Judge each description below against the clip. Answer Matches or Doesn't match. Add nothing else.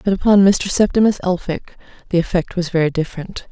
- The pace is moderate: Matches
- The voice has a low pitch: Doesn't match